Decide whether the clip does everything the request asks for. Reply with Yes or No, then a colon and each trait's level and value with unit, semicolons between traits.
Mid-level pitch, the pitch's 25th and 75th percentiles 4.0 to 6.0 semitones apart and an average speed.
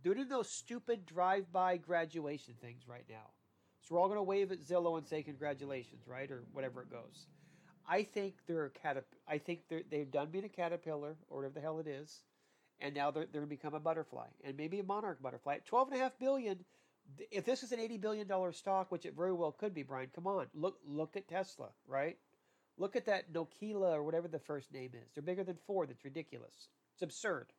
No: medium, 165 Hz; average, 4.9 semitones; fast, 220 wpm